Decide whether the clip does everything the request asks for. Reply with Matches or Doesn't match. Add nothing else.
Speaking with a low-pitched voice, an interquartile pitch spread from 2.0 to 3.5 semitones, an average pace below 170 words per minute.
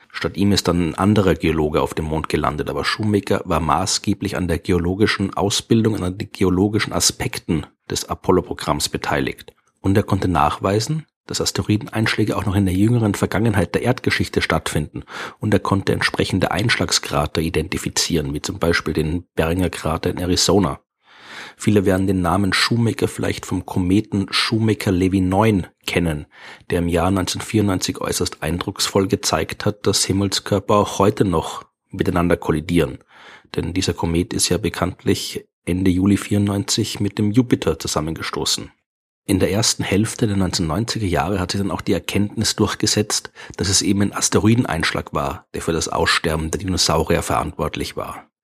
Matches